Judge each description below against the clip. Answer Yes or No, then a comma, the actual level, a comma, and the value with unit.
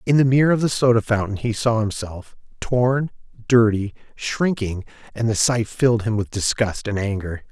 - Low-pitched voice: Yes, low, 115 Hz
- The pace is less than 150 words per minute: No, average, 175 wpm